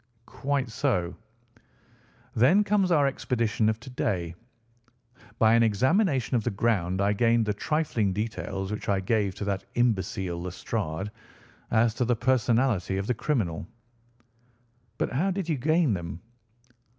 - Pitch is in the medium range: No, low, 110 Hz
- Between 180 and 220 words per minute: No, average, 140 wpm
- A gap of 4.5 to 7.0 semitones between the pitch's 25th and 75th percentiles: Yes, average, 5.1 semitones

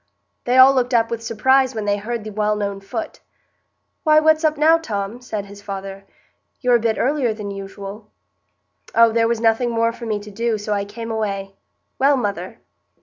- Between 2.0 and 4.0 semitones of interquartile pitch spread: Yes, average, 3.3 semitones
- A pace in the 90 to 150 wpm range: No, average, 195 wpm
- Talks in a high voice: Yes, high, 225 Hz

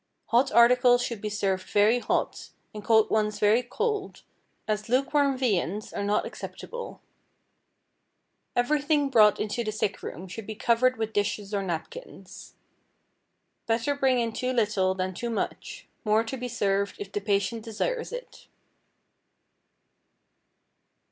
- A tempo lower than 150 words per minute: Yes, slow, 135 wpm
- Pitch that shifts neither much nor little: Yes, average, 3.5 semitones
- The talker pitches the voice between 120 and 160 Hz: No, high, 225 Hz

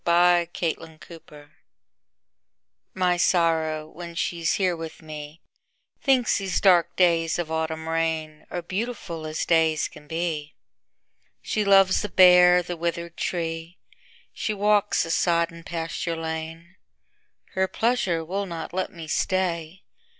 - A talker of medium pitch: Yes, medium, 170 Hz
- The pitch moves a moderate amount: No, narrow, 2.0 semitones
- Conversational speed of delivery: No, slow, 115 wpm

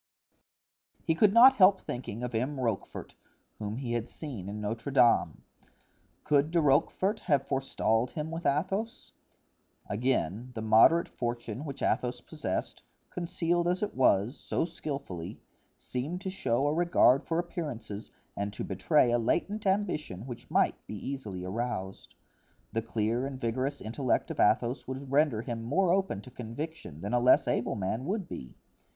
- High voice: No, low, 130 Hz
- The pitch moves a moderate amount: No, wide, 6.1 semitones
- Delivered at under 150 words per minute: No, average, 155 wpm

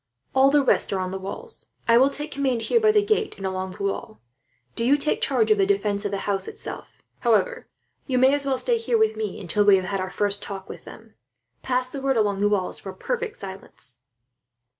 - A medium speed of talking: No, fast, 230 wpm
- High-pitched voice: Yes, very high, 250 Hz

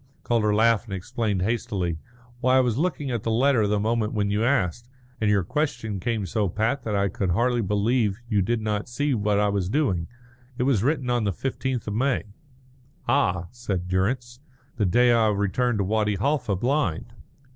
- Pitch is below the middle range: Yes, low, 110 Hz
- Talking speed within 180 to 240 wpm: Yes, average, 190 wpm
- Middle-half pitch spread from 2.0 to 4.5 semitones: Yes, average, 3.4 semitones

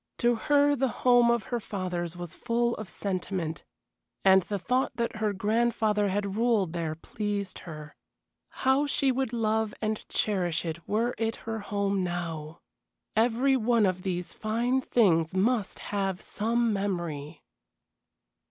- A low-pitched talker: No, high, 210 Hz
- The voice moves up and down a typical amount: Yes, average, 4.5 semitones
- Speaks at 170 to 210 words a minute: No, average, 145 wpm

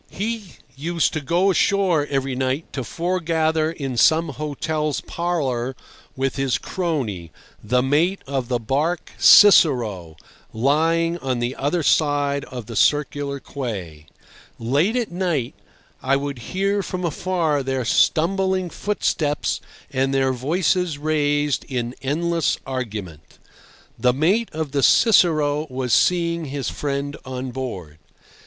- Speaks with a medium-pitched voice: Yes, medium, 145 Hz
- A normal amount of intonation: Yes, average, 4.4 semitones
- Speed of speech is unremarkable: No, slow, 125 wpm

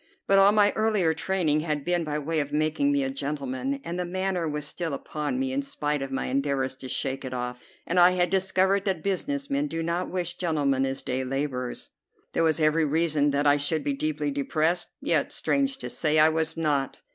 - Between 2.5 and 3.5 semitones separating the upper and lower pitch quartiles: No, average, 4.6 semitones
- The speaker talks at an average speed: No, fast, 215 wpm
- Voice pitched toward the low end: No, medium, 160 Hz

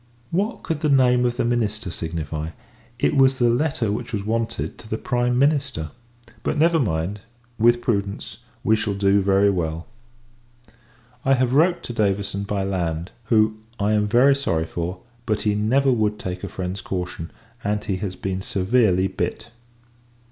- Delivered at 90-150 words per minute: No, average, 165 wpm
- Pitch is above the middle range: No, low, 105 Hz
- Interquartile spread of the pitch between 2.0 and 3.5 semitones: No, average, 4.4 semitones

